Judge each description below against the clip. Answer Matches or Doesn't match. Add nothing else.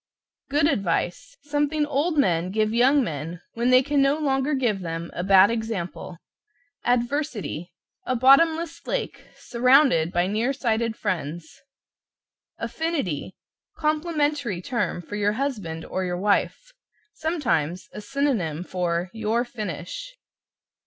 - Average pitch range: Doesn't match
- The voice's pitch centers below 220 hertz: Doesn't match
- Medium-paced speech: Doesn't match